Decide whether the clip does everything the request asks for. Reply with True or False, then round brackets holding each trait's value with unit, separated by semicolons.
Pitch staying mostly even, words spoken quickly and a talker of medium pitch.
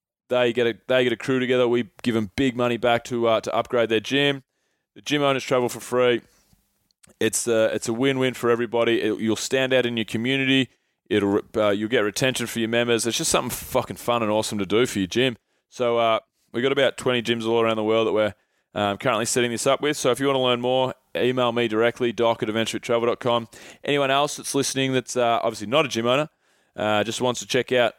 False (2.3 semitones; 240 wpm; 120 Hz)